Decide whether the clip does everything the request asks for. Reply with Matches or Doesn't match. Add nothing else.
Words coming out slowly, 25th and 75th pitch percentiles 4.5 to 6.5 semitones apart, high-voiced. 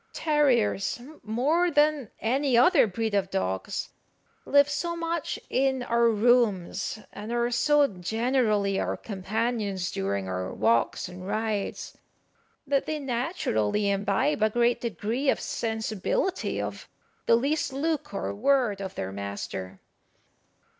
Matches